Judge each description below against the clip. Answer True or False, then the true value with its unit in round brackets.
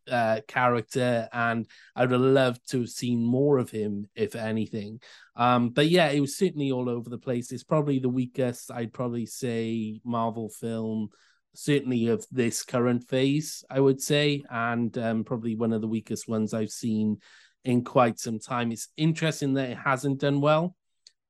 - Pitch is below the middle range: True (120 Hz)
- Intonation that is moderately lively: True (3.1 semitones)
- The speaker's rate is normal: True (175 wpm)